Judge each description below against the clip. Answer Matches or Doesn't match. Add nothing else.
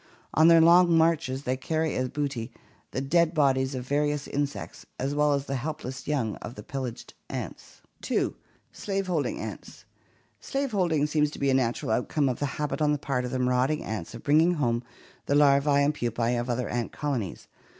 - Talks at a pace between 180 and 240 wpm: Matches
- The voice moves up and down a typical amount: Matches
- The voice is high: Doesn't match